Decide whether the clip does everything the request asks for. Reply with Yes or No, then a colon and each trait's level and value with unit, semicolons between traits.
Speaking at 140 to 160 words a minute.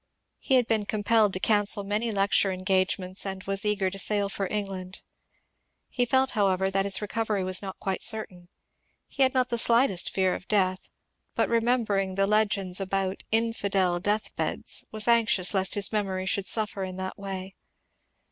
No: average, 175 wpm